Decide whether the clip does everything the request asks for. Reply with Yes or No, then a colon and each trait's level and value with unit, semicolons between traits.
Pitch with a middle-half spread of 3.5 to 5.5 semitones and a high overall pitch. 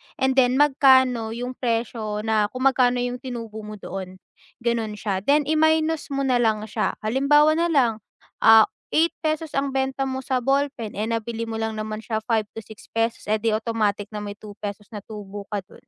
Yes: average, 3.8 semitones; high, 230 Hz